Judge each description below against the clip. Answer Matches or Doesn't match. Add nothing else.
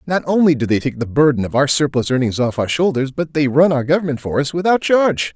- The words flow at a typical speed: Doesn't match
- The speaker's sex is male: Matches